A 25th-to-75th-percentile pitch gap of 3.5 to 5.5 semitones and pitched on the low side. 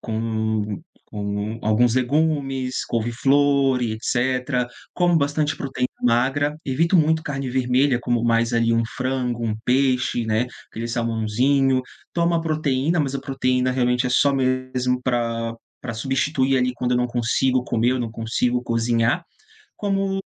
No: average, 2.7 semitones; low, 125 Hz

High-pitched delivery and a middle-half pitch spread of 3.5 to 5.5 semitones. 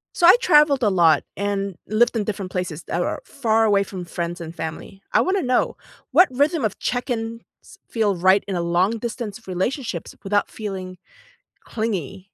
Yes: high, 205 Hz; average, 4.4 semitones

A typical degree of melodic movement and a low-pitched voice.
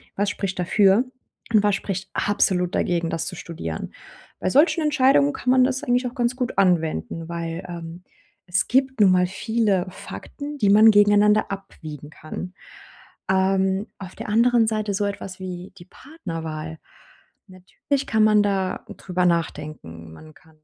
No: average, 4.1 semitones; high, 190 Hz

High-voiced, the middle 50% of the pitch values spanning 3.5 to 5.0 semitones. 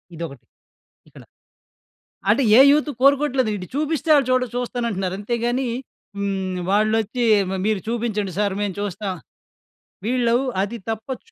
Yes: high, 225 Hz; average, 4.1 semitones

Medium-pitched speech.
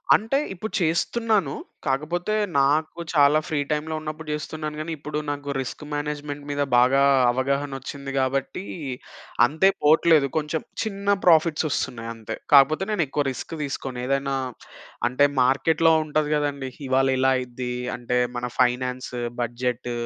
Yes: medium, 145 Hz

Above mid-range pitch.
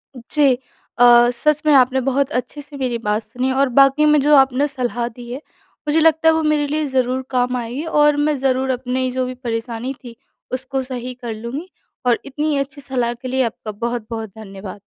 Yes: very high, 260 Hz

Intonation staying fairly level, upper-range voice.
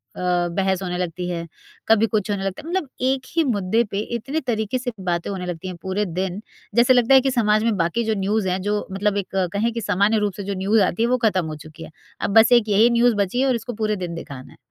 No: average, 4.2 semitones; high, 205 Hz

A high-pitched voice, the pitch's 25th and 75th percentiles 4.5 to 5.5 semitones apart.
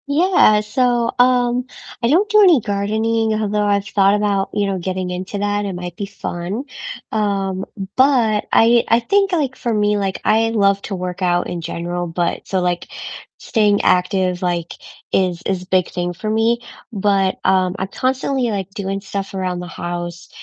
No: high, 200 Hz; average, 3.7 semitones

